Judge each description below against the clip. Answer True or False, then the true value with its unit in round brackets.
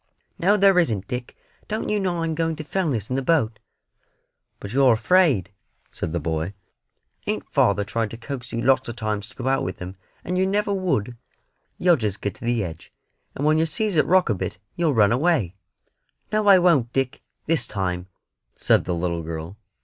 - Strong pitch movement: True (8.8 semitones)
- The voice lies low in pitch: True (125 Hz)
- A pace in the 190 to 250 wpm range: True (195 wpm)